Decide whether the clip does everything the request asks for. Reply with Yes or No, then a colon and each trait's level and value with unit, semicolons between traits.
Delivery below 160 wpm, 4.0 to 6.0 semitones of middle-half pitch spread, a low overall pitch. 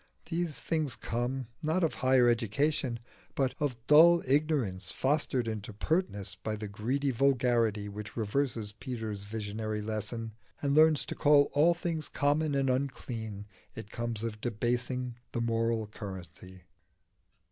Yes: slow, 135 wpm; average, 4.9 semitones; low, 120 Hz